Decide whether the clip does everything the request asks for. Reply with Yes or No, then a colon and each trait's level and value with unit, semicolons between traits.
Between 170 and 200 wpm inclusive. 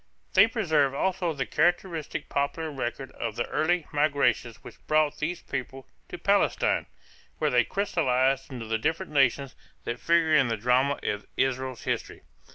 No: average, 155 wpm